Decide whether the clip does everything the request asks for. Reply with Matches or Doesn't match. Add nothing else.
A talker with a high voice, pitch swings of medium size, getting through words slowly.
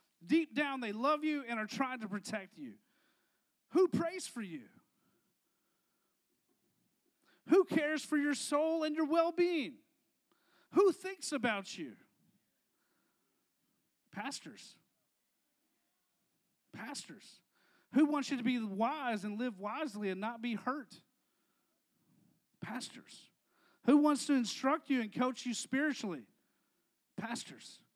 Matches